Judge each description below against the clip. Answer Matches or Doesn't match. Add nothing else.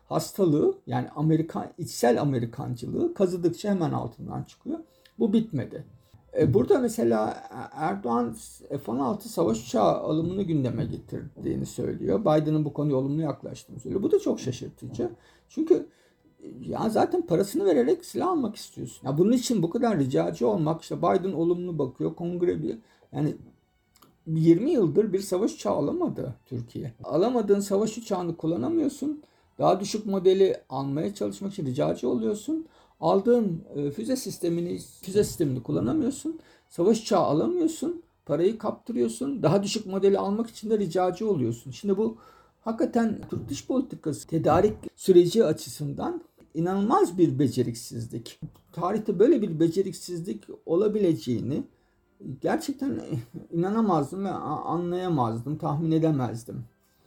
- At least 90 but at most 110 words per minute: Doesn't match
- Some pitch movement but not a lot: Doesn't match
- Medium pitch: Matches